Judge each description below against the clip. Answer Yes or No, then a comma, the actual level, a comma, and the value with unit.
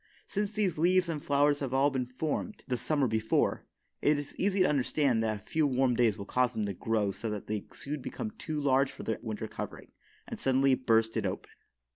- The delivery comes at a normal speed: No, fast, 215 wpm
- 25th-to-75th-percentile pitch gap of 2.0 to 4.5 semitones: No, average, 5.0 semitones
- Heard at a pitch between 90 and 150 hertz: Yes, low, 135 Hz